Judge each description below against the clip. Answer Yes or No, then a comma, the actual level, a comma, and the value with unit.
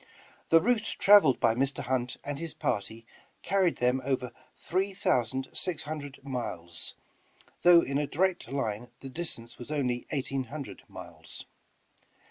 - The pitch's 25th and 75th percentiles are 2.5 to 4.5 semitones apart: No, average, 4.9 semitones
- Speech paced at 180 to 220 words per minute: No, average, 140 wpm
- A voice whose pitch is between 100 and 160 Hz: Yes, low, 135 Hz